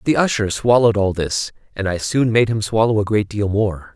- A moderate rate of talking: No, fast, 225 wpm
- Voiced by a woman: No, male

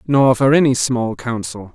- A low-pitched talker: Yes, low, 125 Hz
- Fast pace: No, average, 170 wpm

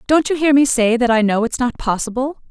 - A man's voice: No, female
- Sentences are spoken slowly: No, fast, 265 wpm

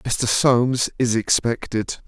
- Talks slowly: Yes, slow, 115 wpm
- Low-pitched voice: Yes, low, 120 Hz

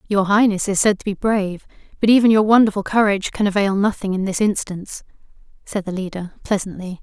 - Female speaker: Yes, female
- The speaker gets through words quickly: No, average, 190 wpm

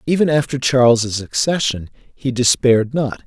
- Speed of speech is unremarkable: No, slow, 130 wpm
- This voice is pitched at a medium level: No, low, 130 Hz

